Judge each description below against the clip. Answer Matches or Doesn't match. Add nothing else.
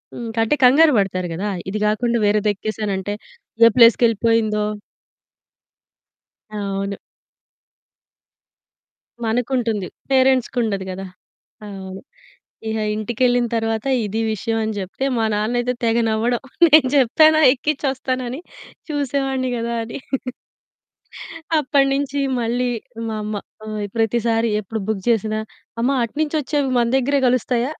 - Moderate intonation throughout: Matches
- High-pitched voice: Matches